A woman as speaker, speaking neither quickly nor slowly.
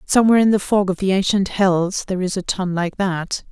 No: female; fast, 240 wpm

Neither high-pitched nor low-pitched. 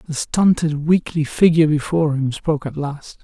Yes: medium, 155 Hz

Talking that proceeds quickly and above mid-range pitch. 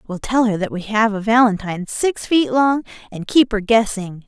Yes: fast, 210 wpm; high, 220 Hz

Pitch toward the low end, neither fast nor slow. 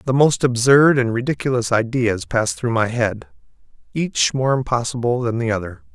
Yes: low, 120 Hz; average, 160 wpm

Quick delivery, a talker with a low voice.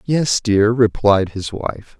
No: average, 150 wpm; low, 110 Hz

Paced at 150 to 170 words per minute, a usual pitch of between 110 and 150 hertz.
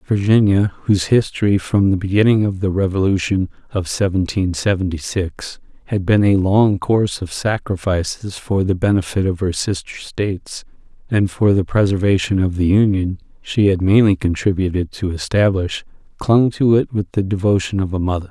No: average, 160 wpm; low, 100 Hz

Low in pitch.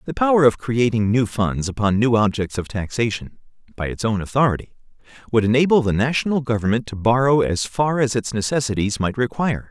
Yes: low, 120 Hz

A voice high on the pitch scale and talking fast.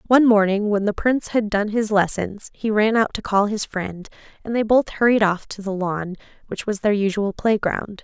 Yes: high, 210 Hz; fast, 215 wpm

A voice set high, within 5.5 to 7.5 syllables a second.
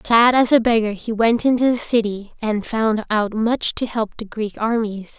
No: high, 225 Hz; 4.4 syllables/s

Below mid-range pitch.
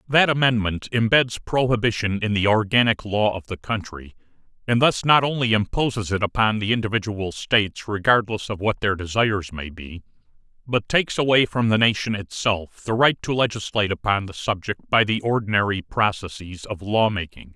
Yes: low, 105 Hz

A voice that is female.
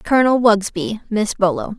Yes: female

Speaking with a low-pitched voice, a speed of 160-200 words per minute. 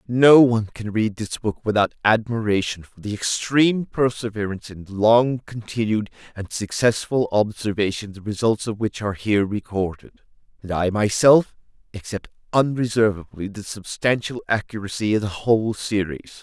No: low, 110 Hz; slow, 135 wpm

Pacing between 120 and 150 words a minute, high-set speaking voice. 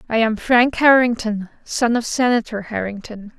Yes: average, 140 wpm; high, 230 Hz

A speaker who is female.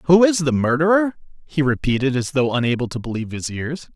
No: male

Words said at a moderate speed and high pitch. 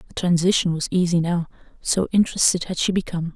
No: average, 180 wpm; medium, 175 Hz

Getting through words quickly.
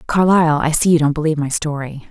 Yes: fast, 230 wpm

